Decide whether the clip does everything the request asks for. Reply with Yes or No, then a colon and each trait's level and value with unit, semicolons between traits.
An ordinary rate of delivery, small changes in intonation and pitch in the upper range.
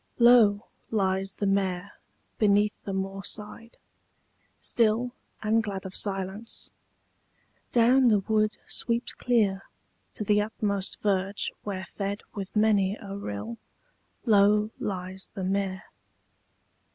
No: slow, 110 wpm; narrow, 2.0 semitones; high, 200 Hz